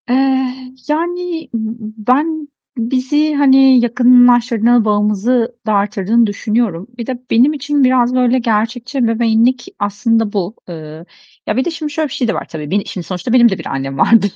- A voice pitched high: Yes, high, 235 Hz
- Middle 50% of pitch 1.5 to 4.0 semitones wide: Yes, average, 3.6 semitones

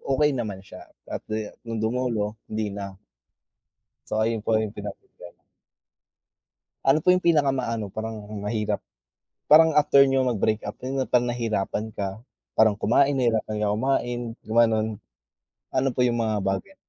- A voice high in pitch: No, low, 115 Hz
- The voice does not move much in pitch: No, average, 3.3 semitones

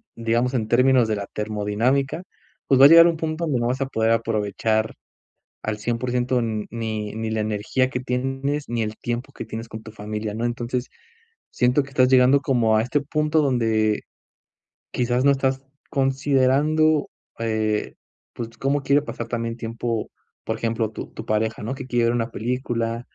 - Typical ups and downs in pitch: Yes, average, 3.1 semitones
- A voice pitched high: No, low, 120 Hz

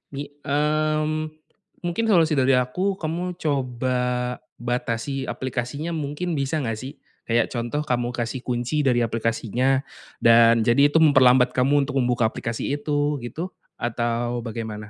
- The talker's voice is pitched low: Yes, low, 130 Hz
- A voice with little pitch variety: No, average, 3.9 semitones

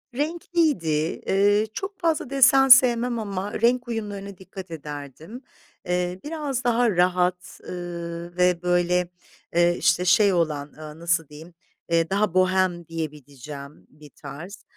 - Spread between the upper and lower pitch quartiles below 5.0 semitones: No, wide, 5.4 semitones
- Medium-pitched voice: Yes, medium, 180 Hz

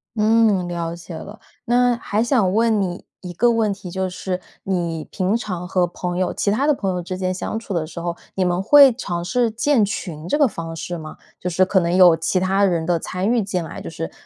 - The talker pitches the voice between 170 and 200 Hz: Yes, medium, 185 Hz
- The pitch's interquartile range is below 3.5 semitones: No, average, 3.9 semitones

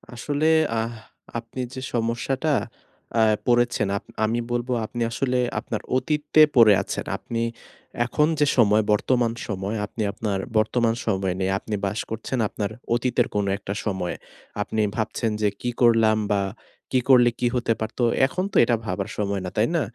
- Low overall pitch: Yes, low, 115 Hz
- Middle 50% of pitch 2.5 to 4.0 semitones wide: Yes, average, 2.8 semitones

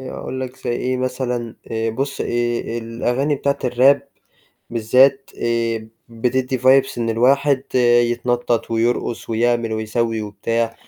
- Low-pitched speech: Yes, low, 120 Hz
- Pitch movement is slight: Yes, narrow, 2.2 semitones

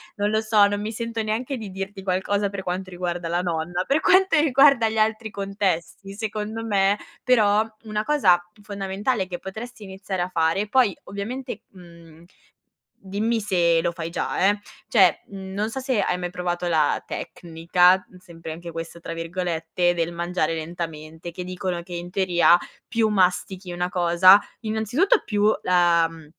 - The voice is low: No, high, 190 Hz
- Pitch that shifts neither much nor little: Yes, average, 3.5 semitones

